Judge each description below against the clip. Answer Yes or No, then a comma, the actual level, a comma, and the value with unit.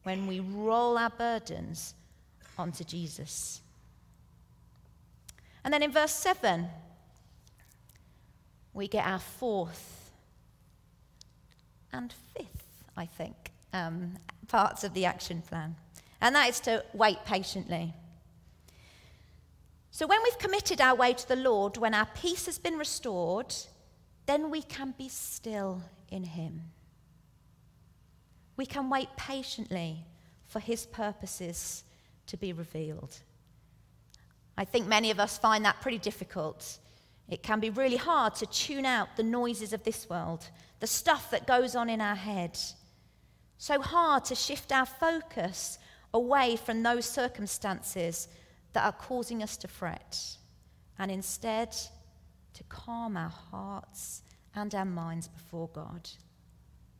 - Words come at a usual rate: No, slow, 125 wpm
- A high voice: Yes, high, 205 Hz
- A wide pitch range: Yes, wide, 6.3 semitones